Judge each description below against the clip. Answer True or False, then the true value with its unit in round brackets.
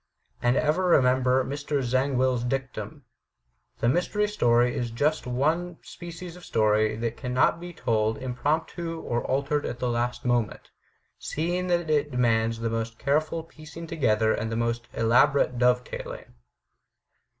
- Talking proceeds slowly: False (150 wpm)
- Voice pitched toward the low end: True (130 Hz)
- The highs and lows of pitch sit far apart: False (4.7 semitones)